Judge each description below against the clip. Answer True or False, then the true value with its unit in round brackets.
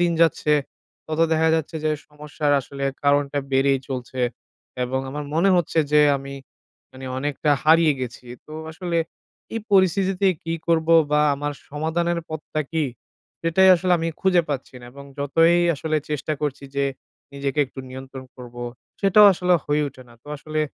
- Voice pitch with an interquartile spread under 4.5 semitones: True (3.2 semitones)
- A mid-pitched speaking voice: True (150 Hz)